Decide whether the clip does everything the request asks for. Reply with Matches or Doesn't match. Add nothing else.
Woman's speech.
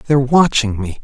Doesn't match